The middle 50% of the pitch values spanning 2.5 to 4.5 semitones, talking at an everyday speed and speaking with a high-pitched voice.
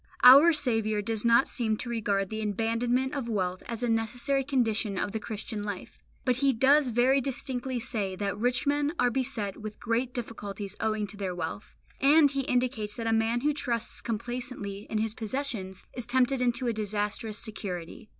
Yes: average, 3.2 semitones; average, 180 wpm; high, 230 Hz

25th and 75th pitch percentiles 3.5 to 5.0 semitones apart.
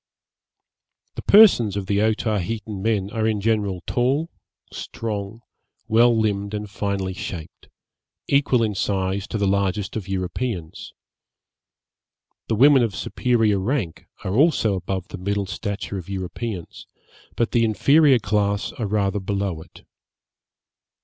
No: average, 2.8 semitones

